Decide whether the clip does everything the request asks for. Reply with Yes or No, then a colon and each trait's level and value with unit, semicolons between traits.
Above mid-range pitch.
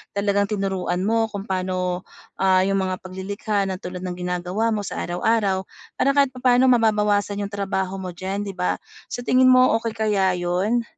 Yes: high, 195 Hz